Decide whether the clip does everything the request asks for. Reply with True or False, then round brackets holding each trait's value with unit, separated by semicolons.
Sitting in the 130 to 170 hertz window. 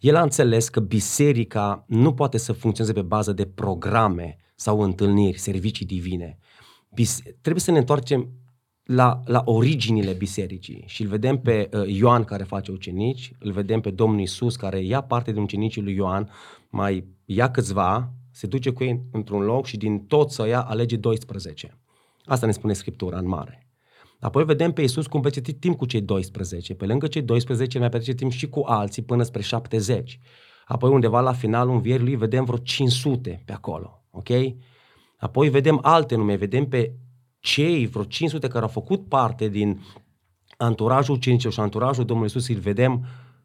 False (115 Hz)